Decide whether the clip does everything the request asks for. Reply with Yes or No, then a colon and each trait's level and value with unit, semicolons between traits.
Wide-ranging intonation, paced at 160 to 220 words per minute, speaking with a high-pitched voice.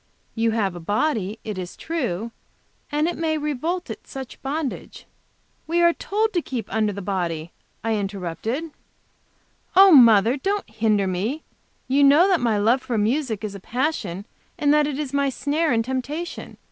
Yes: wide, 6.4 semitones; average, 170 wpm; very high, 250 Hz